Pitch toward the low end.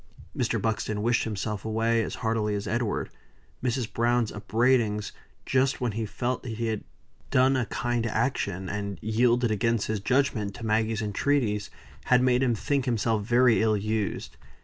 Yes: low, 115 Hz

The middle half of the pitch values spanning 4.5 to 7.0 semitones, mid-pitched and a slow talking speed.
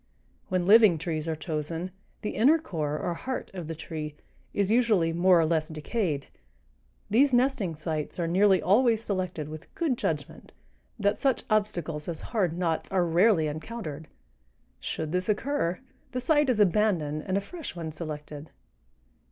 No: wide, 5.4 semitones; medium, 180 Hz; average, 160 wpm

